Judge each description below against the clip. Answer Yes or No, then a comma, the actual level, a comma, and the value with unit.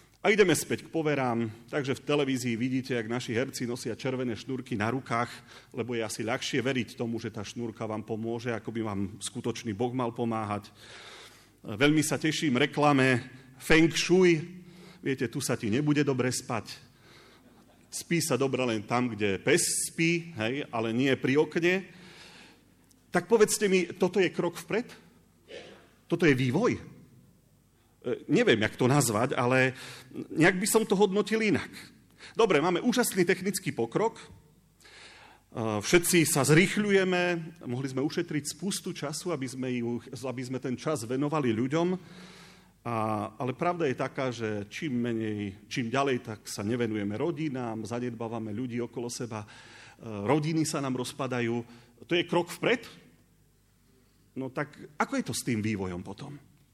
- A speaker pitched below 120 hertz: No, low, 130 Hz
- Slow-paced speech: No, average, 145 wpm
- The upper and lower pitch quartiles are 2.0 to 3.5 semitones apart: No, wide, 5.4 semitones